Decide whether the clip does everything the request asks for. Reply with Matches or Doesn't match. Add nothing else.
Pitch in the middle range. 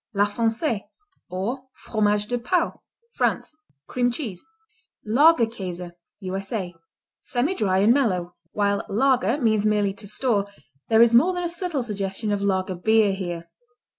Doesn't match